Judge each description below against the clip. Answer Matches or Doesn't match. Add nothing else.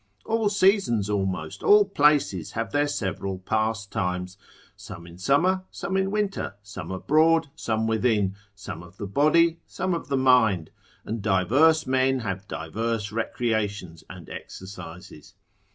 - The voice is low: Matches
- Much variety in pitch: Matches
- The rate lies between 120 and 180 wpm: Matches